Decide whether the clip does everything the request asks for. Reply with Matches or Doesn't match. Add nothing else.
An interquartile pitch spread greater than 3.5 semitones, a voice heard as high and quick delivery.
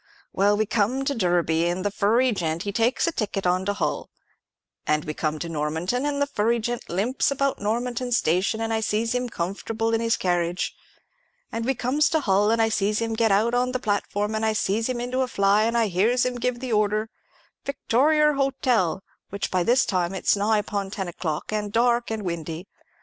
Matches